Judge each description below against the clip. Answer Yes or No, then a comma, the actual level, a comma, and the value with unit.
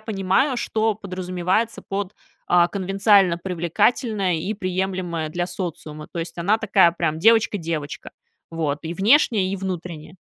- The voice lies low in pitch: No, medium, 185 Hz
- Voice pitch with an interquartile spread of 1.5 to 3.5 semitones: Yes, average, 3.2 semitones